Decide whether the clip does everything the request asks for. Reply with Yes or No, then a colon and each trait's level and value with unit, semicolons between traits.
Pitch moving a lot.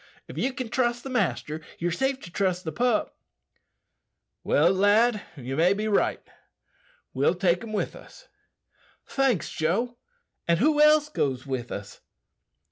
Yes: wide, 7.3 semitones